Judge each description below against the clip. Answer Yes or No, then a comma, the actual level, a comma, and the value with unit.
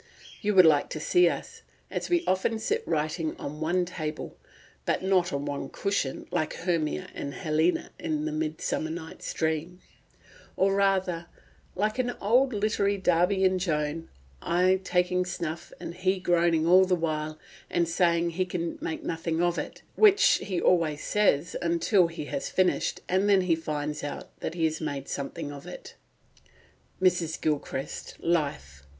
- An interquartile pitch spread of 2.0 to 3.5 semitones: Yes, average, 3.2 semitones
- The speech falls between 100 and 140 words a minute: No, average, 165 wpm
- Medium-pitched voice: Yes, medium, 170 Hz